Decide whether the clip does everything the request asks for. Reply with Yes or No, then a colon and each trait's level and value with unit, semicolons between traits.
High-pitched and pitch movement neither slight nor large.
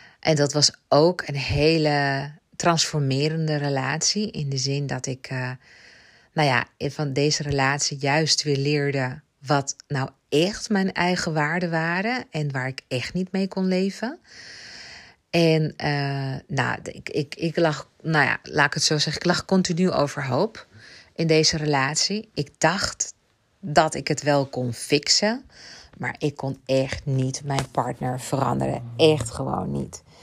No: medium, 145 Hz; average, 3.1 semitones